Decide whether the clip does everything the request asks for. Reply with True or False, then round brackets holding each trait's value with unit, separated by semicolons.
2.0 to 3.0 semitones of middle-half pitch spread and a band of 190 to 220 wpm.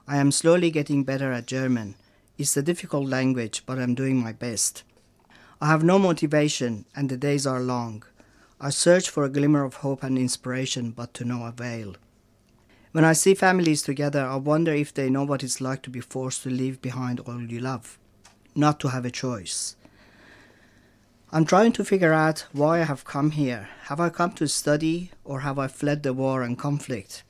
False (3.4 semitones; 195 wpm)